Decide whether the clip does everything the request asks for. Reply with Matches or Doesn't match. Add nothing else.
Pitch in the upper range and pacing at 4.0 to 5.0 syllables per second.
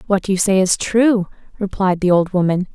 Matches